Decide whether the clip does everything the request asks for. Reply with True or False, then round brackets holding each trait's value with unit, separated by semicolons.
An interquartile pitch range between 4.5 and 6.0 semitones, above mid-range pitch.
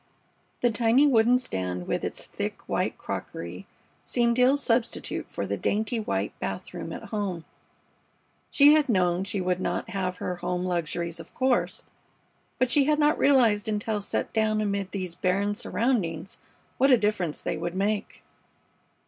True (5.2 semitones; 205 Hz)